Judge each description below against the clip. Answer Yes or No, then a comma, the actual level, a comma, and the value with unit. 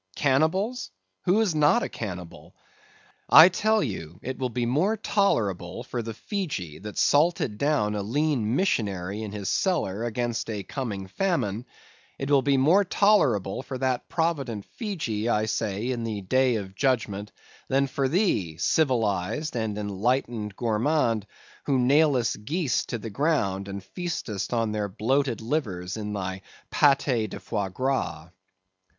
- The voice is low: Yes, low, 120 Hz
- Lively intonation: Yes, wide, 6.1 semitones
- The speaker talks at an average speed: Yes, average, 145 wpm